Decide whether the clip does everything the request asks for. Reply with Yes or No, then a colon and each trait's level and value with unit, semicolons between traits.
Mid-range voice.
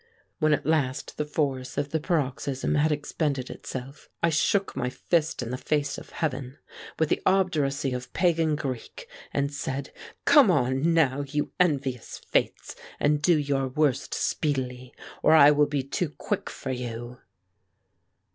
Yes: medium, 145 Hz